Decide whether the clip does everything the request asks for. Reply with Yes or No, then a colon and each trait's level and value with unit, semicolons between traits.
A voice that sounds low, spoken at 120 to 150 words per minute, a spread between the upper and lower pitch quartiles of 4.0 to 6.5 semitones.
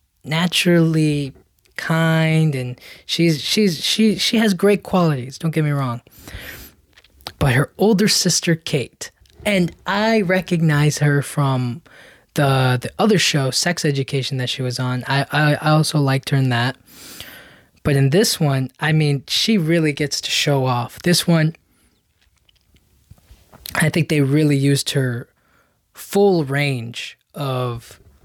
No: medium, 145 Hz; average, 140 wpm; average, 4.4 semitones